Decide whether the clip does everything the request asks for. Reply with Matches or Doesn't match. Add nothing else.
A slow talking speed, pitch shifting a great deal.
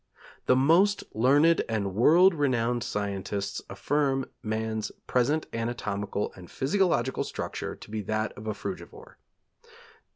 Matches